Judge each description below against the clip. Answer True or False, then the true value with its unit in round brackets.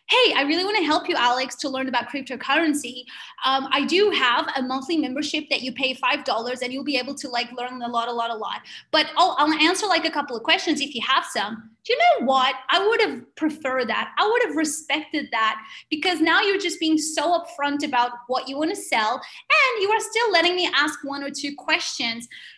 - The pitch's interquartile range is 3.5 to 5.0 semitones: True (4.5 semitones)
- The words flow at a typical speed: False (230 wpm)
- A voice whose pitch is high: True (285 Hz)